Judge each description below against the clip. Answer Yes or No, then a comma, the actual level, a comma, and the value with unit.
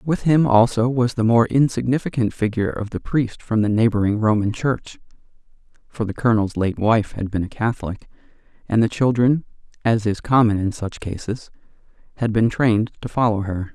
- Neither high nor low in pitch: No, low, 110 Hz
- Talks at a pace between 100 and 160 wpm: No, average, 175 wpm